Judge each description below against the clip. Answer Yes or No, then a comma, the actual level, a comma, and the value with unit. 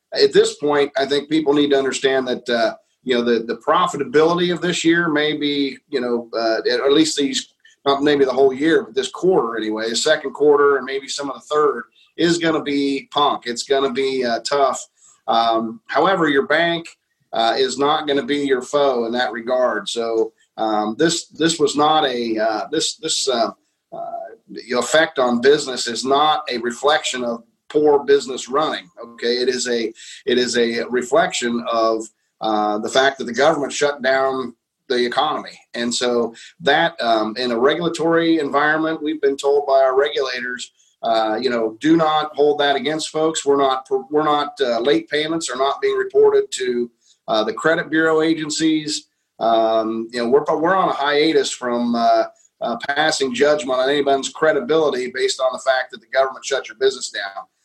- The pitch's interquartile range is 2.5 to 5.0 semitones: Yes, average, 4.4 semitones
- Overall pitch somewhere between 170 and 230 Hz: No, medium, 140 Hz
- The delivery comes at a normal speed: Yes, average, 185 wpm